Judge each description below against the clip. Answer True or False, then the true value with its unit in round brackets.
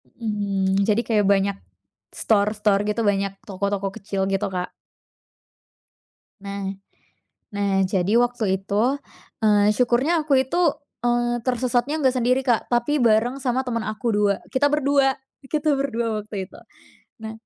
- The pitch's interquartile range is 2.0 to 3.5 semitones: False (3.9 semitones)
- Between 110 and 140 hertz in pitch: False (220 Hz)